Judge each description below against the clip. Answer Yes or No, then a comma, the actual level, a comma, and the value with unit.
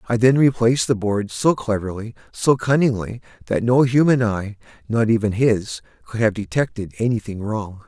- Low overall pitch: Yes, low, 110 Hz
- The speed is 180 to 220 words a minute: No, average, 150 wpm